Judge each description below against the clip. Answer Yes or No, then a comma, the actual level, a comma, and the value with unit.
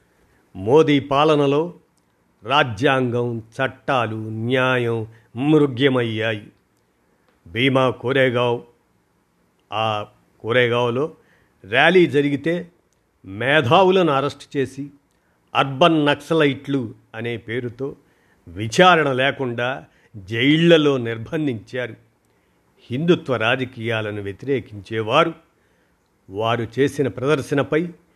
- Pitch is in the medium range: No, low, 130 Hz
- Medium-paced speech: No, slow, 60 wpm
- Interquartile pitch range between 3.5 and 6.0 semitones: Yes, average, 4.3 semitones